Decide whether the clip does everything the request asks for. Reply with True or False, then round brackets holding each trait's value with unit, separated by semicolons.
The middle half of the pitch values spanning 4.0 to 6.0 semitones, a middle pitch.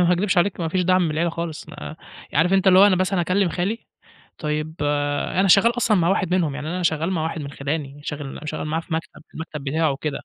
False (3.4 semitones; 165 Hz)